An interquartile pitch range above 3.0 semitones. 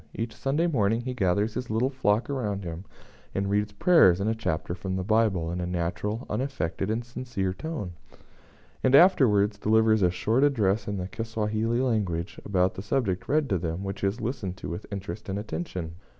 Yes: average, 4.1 semitones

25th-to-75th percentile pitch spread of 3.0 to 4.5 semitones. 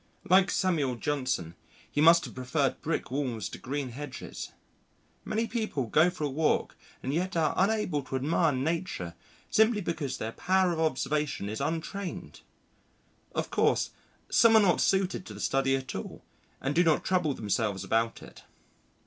No: wide, 5.5 semitones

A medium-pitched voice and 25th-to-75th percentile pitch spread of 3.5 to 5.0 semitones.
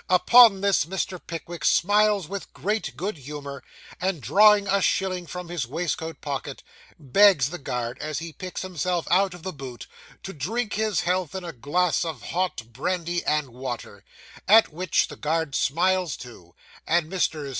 Yes: medium, 175 Hz; average, 4.7 semitones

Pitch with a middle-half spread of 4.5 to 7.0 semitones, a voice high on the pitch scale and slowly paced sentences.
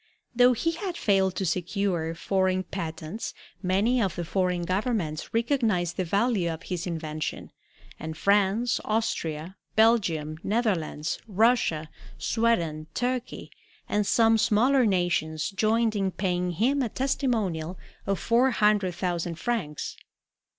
Yes: average, 5.1 semitones; high, 195 Hz; slow, 120 wpm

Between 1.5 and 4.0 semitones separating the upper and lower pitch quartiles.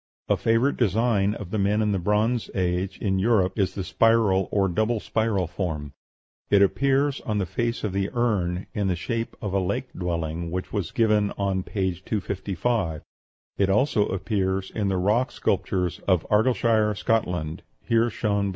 Yes: average, 3.2 semitones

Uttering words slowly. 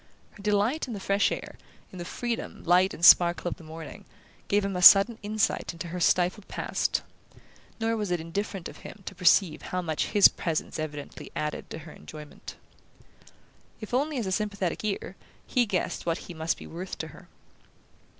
No: average, 185 wpm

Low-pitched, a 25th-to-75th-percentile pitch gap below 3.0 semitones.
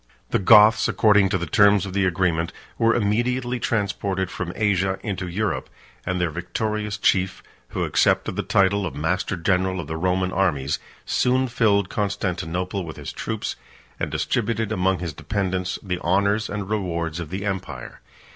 Yes: very low, 95 Hz; narrow, 2.5 semitones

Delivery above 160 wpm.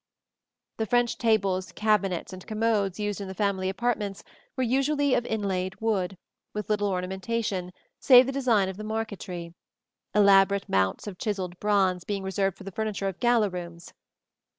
Yes: average, 170 wpm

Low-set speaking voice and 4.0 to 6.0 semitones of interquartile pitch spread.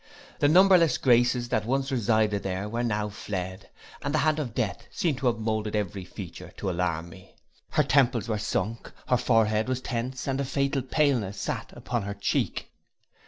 Yes: low, 115 Hz; average, 4.3 semitones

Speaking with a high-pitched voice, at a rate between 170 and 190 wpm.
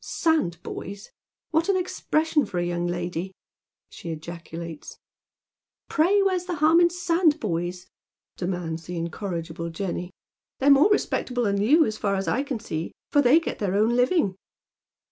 Yes: high, 205 Hz; average, 175 wpm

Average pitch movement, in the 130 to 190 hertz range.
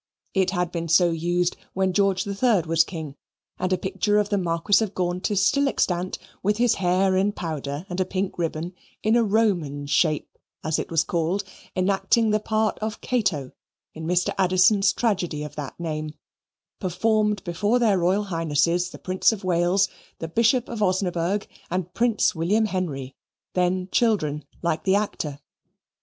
Yes: average, 3.5 semitones; medium, 185 Hz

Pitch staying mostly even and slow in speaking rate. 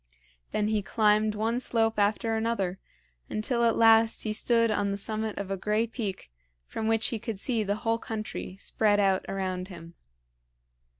No: narrow, 2.0 semitones; average, 170 wpm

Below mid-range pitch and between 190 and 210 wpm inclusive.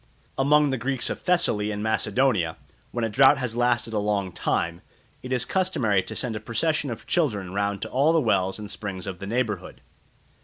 Yes: low, 110 Hz; average, 195 wpm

